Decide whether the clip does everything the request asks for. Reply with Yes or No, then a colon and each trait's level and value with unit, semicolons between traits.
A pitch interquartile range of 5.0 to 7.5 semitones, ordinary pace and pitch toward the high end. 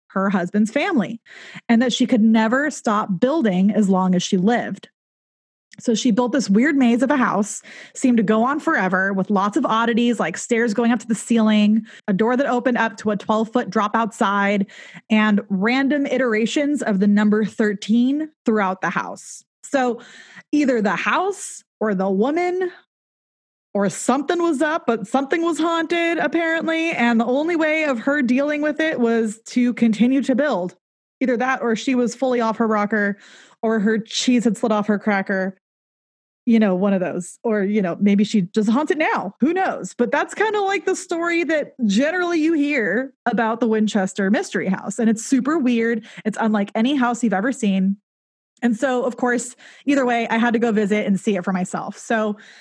No: average, 4.4 semitones; average, 190 wpm; high, 230 Hz